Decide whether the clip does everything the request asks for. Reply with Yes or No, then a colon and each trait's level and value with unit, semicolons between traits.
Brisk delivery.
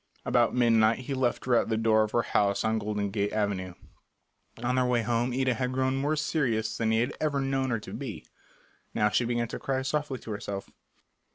Yes: fast, 210 wpm